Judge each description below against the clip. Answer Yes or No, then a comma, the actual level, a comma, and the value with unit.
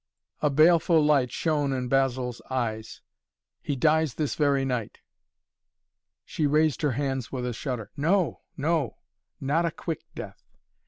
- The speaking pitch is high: No, medium, 140 Hz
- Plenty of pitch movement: No, average, 3.5 semitones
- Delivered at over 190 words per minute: No, average, 140 wpm